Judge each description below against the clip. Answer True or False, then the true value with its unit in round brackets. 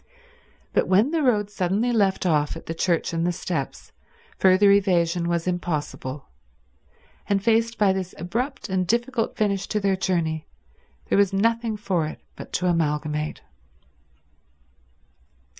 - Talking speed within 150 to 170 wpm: False (140 wpm)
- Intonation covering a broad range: False (3.8 semitones)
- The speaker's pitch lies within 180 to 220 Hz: True (190 Hz)